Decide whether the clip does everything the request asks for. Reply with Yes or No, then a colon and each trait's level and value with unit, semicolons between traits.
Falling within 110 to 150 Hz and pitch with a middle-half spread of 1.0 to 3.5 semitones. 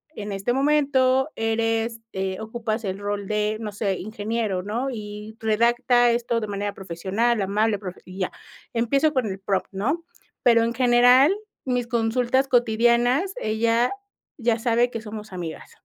No: high, 225 Hz; average, 2.8 semitones